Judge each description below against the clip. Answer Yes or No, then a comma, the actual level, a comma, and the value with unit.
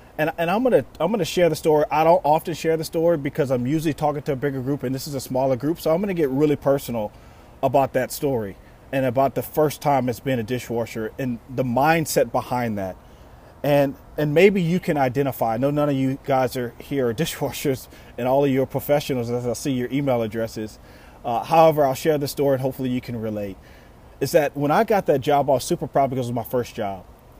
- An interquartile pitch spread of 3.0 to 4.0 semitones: Yes, average, 3.4 semitones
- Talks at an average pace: No, fast, 235 wpm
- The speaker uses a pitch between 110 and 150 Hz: Yes, low, 135 Hz